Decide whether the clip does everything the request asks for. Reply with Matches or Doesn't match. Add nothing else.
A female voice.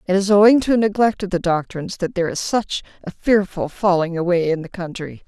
Matches